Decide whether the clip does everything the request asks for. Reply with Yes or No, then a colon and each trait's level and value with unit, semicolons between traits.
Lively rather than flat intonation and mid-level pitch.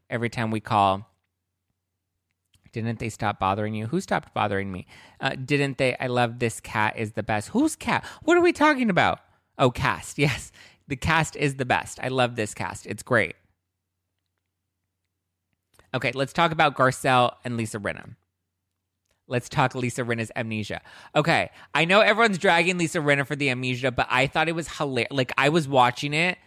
No: wide, 6.6 semitones; low, 120 Hz